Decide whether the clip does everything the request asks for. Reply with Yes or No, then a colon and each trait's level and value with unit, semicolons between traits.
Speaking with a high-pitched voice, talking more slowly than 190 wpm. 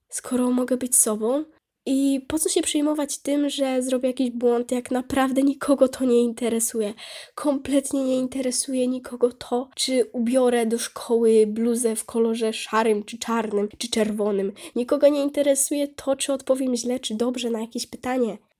Yes: very high, 250 Hz; fast, 160 wpm